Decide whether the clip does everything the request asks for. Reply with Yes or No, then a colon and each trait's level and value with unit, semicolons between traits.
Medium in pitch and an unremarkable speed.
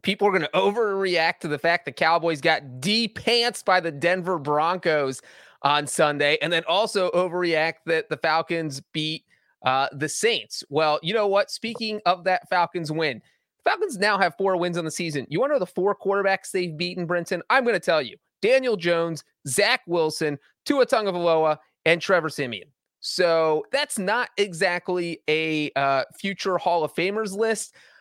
Yes: medium, 175 Hz; average, 175 wpm